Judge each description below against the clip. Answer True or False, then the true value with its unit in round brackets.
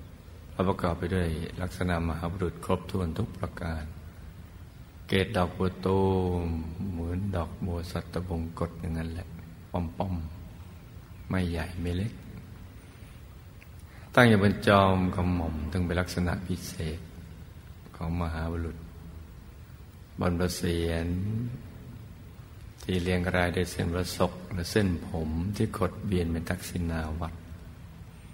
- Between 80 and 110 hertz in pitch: True (90 Hz)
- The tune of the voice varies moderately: False (1.9 semitones)